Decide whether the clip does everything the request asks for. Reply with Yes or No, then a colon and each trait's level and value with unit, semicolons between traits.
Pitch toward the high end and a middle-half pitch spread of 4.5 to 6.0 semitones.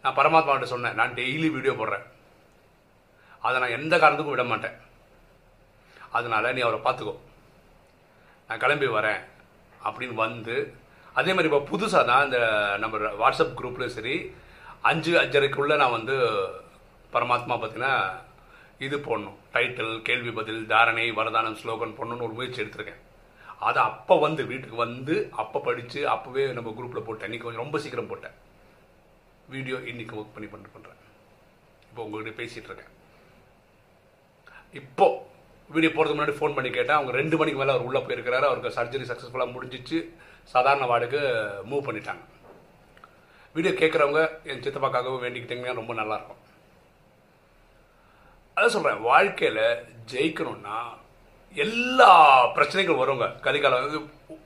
No: low, 135 Hz; average, 5.3 semitones